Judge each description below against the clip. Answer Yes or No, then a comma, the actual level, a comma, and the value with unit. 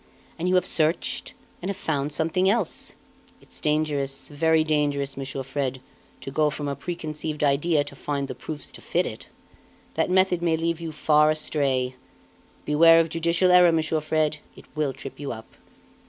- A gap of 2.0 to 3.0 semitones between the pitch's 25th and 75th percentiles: Yes, narrow, 2.6 semitones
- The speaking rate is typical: Yes, average, 170 wpm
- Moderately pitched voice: Yes, medium, 155 Hz